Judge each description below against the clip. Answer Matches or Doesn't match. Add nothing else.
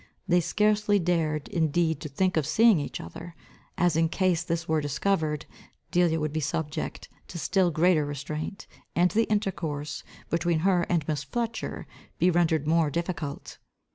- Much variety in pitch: Doesn't match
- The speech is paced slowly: Doesn't match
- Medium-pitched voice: Matches